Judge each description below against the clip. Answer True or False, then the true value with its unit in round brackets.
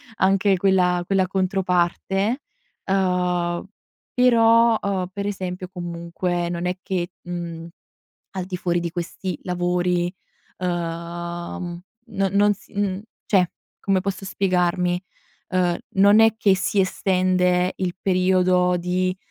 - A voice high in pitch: False (180 Hz)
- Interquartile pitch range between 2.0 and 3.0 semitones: False (1.6 semitones)